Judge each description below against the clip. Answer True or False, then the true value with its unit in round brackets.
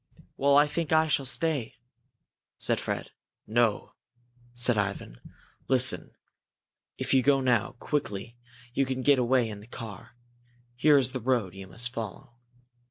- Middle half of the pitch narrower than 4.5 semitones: True (3.7 semitones)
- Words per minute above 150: False (145 wpm)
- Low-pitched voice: True (125 Hz)